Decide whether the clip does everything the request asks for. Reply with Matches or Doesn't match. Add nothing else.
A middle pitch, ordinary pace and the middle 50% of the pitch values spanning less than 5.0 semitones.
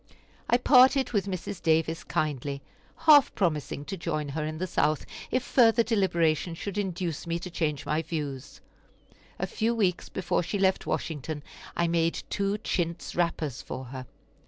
Matches